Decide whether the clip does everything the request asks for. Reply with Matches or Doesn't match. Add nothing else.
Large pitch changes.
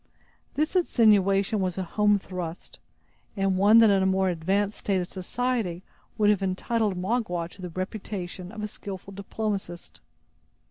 Doesn't match